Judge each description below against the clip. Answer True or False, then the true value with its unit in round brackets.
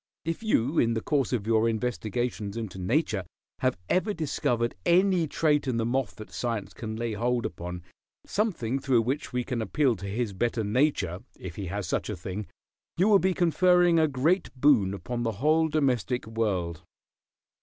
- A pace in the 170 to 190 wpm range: True (175 wpm)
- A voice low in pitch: True (120 Hz)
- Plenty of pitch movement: True (5.8 semitones)